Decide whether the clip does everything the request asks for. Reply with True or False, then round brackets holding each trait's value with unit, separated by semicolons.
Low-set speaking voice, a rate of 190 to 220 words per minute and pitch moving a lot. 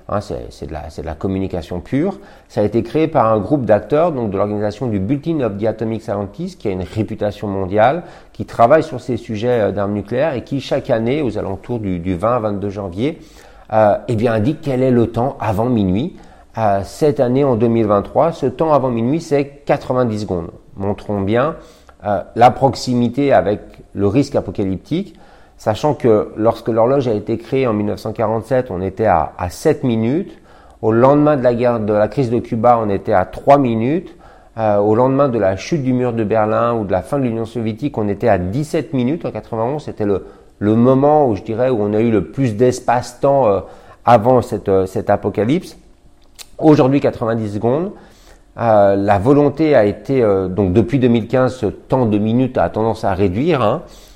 False (115 Hz; 195 wpm; 4.1 semitones)